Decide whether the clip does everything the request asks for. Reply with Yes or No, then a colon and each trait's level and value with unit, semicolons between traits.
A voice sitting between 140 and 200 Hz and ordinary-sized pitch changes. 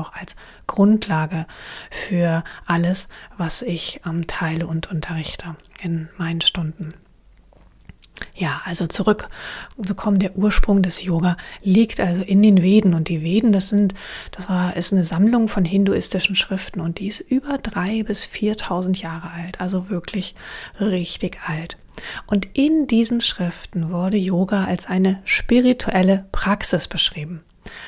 Yes: medium, 185 Hz; average, 3.0 semitones